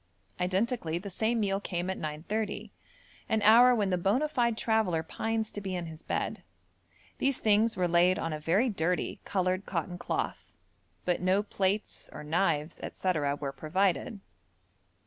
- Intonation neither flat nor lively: Yes, average, 3.9 semitones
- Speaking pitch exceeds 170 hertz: Yes, high, 190 Hz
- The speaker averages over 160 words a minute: No, average, 155 wpm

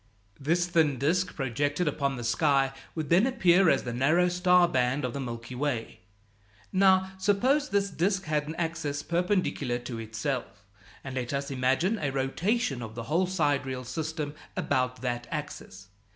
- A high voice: No, medium, 145 Hz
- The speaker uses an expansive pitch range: Yes, wide, 5.7 semitones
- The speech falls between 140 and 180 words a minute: Yes, average, 160 wpm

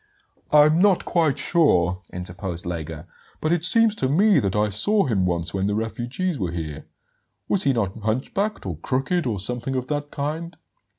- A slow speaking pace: No, average, 175 wpm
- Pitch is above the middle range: No, low, 125 Hz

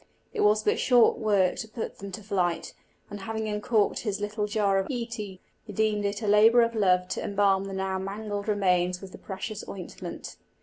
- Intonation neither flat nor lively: No, narrow, 2.0 semitones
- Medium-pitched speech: No, high, 205 Hz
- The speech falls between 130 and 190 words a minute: No, average, 200 wpm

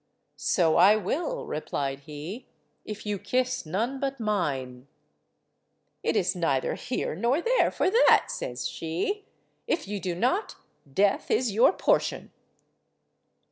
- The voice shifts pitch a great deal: Yes, wide, 8.1 semitones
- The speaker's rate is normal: No, slow, 130 wpm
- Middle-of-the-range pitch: No, high, 205 Hz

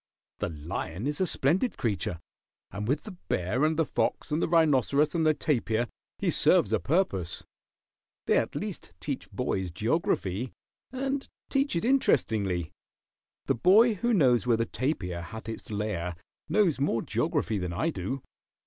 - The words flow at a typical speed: Yes, average, 160 wpm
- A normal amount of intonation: No, wide, 8.7 semitones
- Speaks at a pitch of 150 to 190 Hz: No, low, 130 Hz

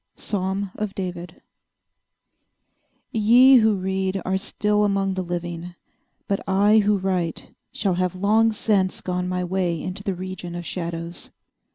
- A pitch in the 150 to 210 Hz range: Yes, high, 190 Hz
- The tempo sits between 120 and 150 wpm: Yes, average, 145 wpm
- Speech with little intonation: Yes, narrow, 2.2 semitones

